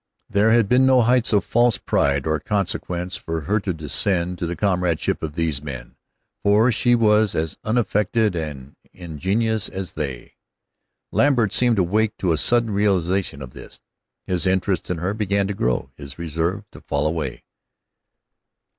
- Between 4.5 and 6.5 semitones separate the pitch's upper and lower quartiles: Yes, average, 5.0 semitones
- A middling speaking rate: Yes, average, 165 wpm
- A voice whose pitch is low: Yes, very low, 95 Hz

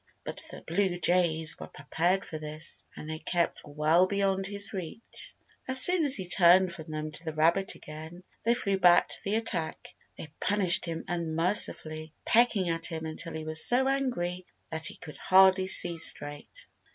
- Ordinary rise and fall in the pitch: Yes, average, 3.5 semitones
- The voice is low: No, medium, 175 Hz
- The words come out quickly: No, average, 175 wpm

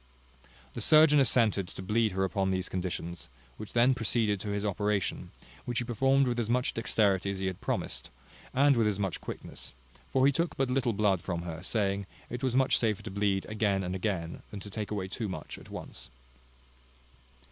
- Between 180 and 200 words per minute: Yes, average, 195 wpm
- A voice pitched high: No, low, 105 Hz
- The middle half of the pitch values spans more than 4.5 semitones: No, average, 4.0 semitones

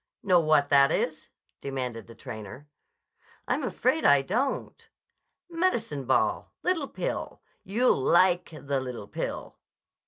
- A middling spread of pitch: No, wide, 8.2 semitones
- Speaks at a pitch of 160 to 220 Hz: No, medium, 150 Hz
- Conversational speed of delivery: No, slow, 120 wpm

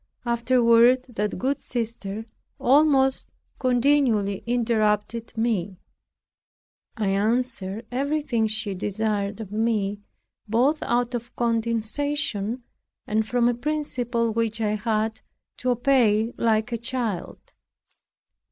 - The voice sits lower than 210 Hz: No, high, 230 Hz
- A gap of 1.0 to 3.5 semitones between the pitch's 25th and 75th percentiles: Yes, narrow, 2.5 semitones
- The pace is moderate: No, slow, 100 wpm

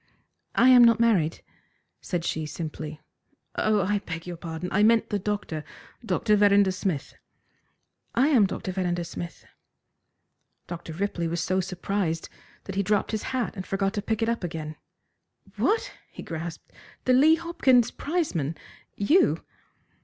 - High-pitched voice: Yes, high, 195 Hz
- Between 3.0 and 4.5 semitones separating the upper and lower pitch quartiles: No, average, 5.0 semitones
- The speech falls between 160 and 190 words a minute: No, average, 145 wpm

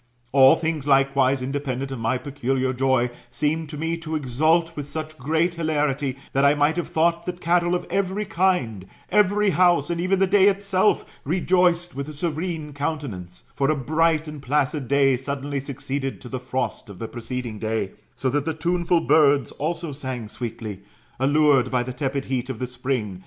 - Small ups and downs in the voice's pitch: No, average, 4.1 semitones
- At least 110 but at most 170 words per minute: No, average, 180 wpm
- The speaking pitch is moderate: Yes, medium, 145 Hz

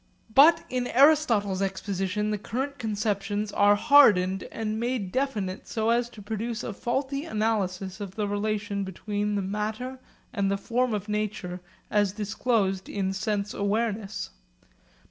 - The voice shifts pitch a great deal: No, average, 2.7 semitones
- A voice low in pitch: No, high, 210 Hz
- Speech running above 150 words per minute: No, average, 140 wpm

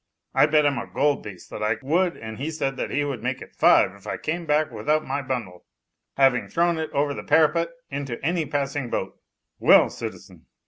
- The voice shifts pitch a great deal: No, average, 3.5 semitones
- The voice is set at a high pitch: No, medium, 145 Hz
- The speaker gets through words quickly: Yes, fast, 210 wpm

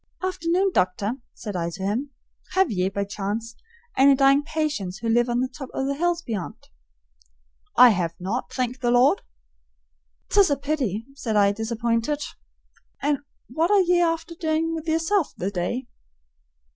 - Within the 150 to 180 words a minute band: Yes, average, 160 wpm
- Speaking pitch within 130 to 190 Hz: No, very high, 255 Hz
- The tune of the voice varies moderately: No, wide, 7.2 semitones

